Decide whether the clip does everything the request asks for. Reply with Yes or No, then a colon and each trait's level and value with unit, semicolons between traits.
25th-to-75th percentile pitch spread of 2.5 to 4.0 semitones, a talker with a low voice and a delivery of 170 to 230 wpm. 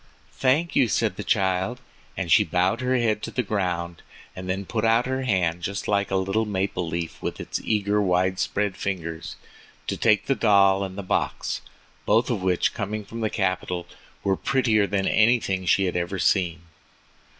Yes: average, 3.1 semitones; low, 100 Hz; average, 185 wpm